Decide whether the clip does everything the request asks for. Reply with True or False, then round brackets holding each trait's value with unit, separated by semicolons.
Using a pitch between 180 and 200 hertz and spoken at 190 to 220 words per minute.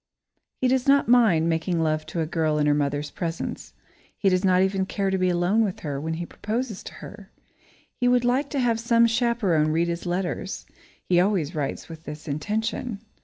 True (185 Hz; 200 wpm)